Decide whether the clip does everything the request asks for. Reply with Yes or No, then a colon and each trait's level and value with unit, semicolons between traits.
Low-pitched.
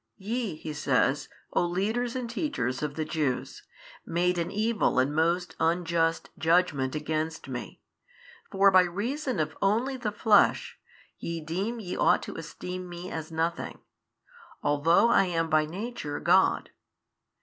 No: medium, 175 Hz